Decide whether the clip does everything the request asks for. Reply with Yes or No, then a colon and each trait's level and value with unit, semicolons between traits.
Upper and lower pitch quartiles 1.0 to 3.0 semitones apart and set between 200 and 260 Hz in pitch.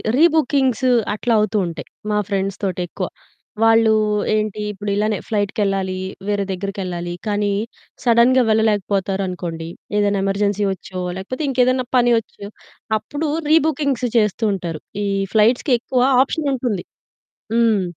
No: average, 3.9 semitones; high, 210 Hz